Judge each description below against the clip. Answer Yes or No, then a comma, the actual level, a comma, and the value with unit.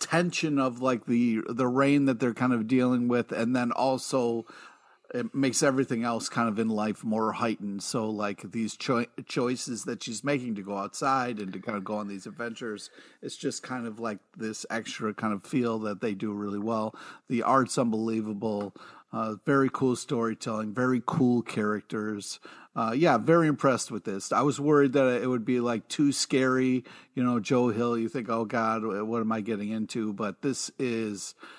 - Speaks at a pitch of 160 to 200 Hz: No, low, 115 Hz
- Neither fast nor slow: Yes, average, 190 wpm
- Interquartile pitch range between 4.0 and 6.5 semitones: No, average, 2.8 semitones